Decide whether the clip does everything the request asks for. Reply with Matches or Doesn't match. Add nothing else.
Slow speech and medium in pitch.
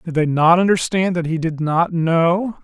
Doesn't match